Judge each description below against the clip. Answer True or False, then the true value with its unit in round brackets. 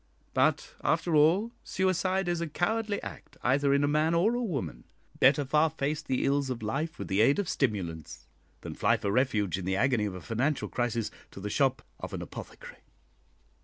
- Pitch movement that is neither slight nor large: False (6.5 semitones)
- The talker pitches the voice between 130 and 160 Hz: True (140 Hz)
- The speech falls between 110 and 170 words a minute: False (195 wpm)